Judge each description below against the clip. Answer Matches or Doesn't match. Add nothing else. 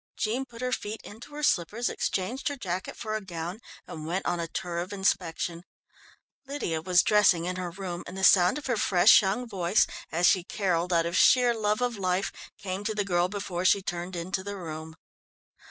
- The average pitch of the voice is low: Doesn't match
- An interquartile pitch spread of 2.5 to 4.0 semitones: Matches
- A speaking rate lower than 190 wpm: Doesn't match